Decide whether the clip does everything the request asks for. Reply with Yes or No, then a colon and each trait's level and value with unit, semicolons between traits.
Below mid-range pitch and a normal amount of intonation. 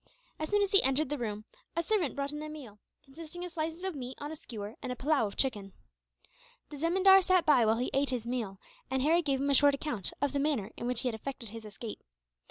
No: very high, 275 Hz; average, 5.0 semitones